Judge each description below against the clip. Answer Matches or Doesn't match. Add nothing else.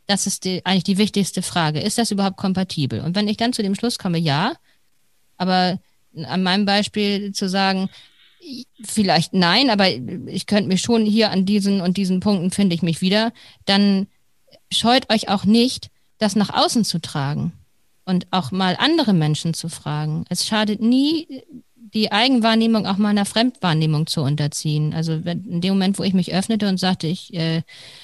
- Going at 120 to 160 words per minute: Doesn't match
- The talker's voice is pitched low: Doesn't match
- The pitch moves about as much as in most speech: Matches